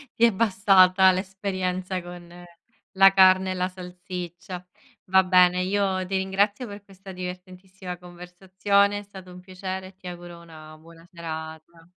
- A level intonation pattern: Yes, narrow, 1.3 semitones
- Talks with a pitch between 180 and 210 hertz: Yes, medium, 185 Hz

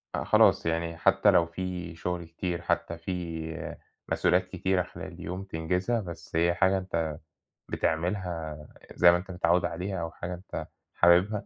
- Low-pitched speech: Yes, very low, 90 Hz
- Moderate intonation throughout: No, narrow, 1.9 semitones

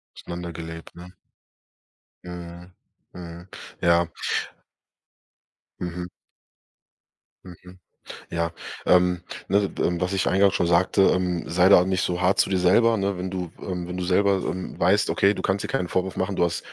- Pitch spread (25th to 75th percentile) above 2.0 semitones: No, narrow, 1.5 semitones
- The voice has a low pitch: Yes, very low, 90 Hz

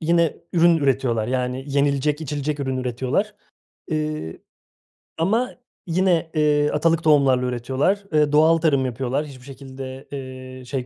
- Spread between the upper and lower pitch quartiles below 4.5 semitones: Yes, average, 3.5 semitones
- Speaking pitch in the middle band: Yes, medium, 145 Hz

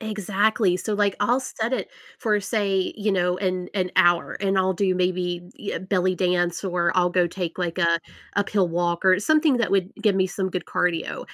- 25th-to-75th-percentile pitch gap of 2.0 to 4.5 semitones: Yes, narrow, 2.5 semitones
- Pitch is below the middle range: No, medium, 185 Hz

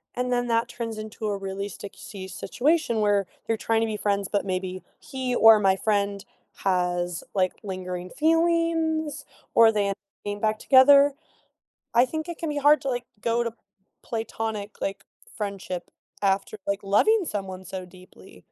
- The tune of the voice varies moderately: Yes, average, 4.3 semitones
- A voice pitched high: Yes, high, 215 Hz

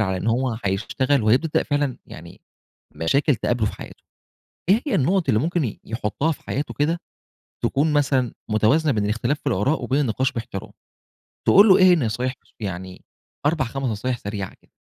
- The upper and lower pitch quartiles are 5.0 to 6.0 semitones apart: Yes, wide, 5.4 semitones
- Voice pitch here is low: Yes, low, 130 Hz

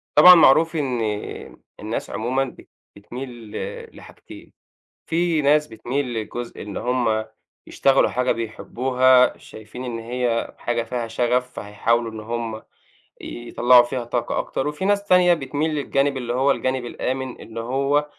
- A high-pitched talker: No, low, 125 Hz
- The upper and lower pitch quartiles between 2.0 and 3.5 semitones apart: Yes, average, 2.8 semitones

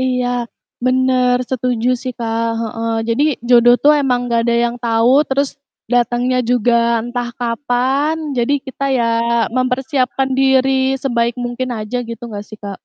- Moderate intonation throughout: No, narrow, 2.0 semitones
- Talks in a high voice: Yes, high, 245 Hz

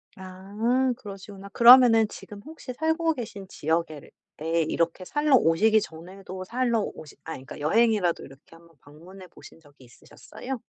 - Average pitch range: No, wide, 6.1 semitones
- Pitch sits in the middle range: No, high, 195 Hz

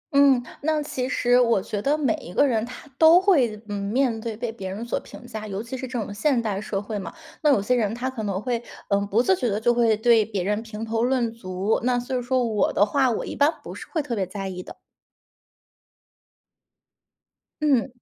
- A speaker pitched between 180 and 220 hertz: No, high, 230 Hz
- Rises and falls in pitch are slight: No, average, 3.5 semitones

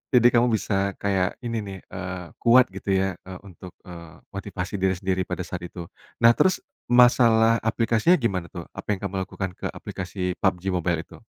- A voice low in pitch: Yes, very low, 95 Hz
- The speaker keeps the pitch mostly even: No, average, 3.9 semitones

